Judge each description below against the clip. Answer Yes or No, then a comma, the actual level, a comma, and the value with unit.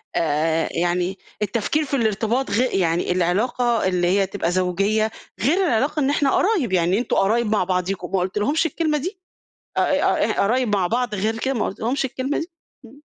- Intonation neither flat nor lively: No, wide, 6.2 semitones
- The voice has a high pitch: Yes, high, 215 Hz